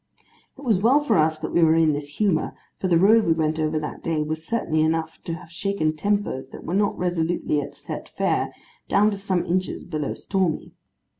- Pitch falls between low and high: Yes, medium, 165 Hz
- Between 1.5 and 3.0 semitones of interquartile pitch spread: No, average, 4.0 semitones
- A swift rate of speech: Yes, fast, 210 wpm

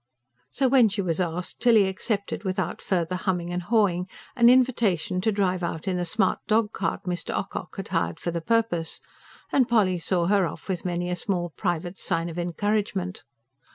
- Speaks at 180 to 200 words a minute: Yes, average, 185 wpm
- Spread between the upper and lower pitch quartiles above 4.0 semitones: No, average, 3.2 semitones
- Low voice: No, medium, 185 Hz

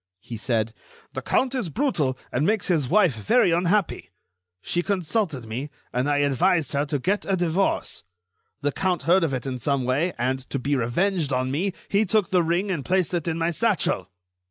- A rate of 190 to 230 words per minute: Yes, average, 195 wpm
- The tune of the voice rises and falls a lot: Yes, wide, 6.1 semitones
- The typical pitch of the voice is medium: Yes, medium, 165 Hz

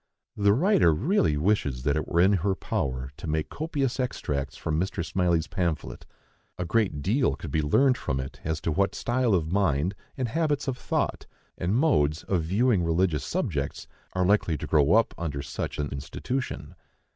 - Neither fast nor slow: Yes, average, 180 wpm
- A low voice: Yes, very low, 90 Hz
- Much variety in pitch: Yes, wide, 6.8 semitones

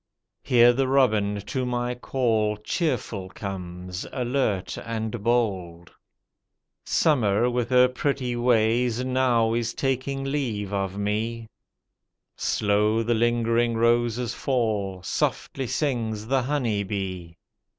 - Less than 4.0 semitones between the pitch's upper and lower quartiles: Yes, average, 3.3 semitones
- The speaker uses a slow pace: Yes, slow, 110 wpm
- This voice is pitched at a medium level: No, low, 115 Hz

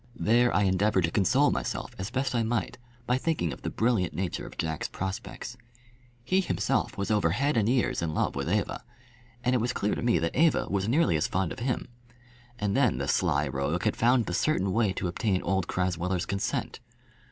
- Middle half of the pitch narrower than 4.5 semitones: No, average, 5.2 semitones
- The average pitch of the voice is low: Yes, low, 100 Hz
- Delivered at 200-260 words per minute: Yes, fast, 205 wpm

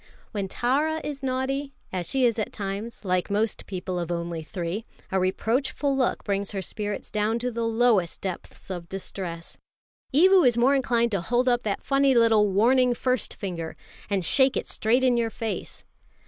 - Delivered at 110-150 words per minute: No, average, 175 wpm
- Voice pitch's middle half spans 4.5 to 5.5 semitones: Yes, average, 4.8 semitones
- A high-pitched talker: Yes, high, 225 Hz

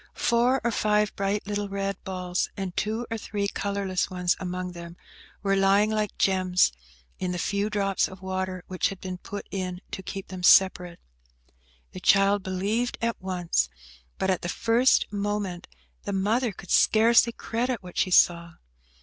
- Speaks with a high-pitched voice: Yes, high, 195 Hz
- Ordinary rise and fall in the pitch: No, narrow, 2.3 semitones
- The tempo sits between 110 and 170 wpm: Yes, average, 165 wpm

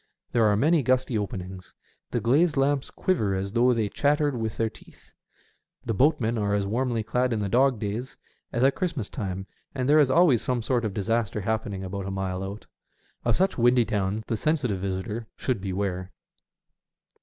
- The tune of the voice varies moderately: Yes, average, 4.4 semitones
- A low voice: Yes, low, 115 Hz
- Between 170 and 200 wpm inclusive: Yes, average, 180 wpm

